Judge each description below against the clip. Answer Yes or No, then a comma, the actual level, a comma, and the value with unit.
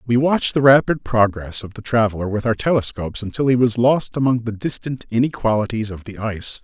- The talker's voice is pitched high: No, low, 115 Hz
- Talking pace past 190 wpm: Yes, average, 200 wpm